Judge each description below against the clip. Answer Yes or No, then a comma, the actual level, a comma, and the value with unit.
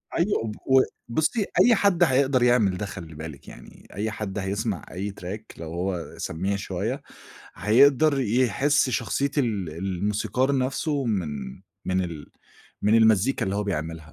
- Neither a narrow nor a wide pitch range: No, wide, 6.1 semitones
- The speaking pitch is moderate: No, low, 105 Hz